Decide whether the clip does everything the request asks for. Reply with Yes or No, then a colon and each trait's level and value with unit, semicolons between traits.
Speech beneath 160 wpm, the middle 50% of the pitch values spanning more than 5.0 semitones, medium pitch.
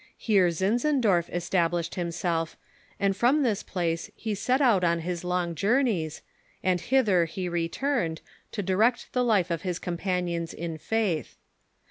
No: average, 140 wpm; average, 4.4 semitones; medium, 180 Hz